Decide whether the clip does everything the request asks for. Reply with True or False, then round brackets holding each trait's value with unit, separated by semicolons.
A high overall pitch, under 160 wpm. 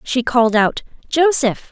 True (255 Hz; 140 wpm)